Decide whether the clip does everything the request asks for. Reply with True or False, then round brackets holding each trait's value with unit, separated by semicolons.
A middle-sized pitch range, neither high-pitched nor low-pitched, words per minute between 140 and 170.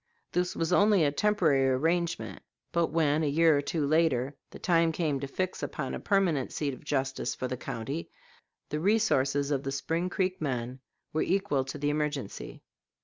False (3.8 semitones; 150 Hz; 180 wpm)